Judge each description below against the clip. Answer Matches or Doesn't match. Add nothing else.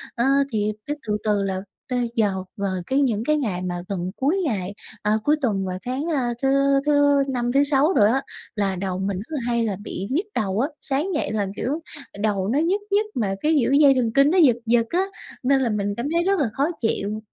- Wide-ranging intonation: Matches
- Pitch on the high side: Matches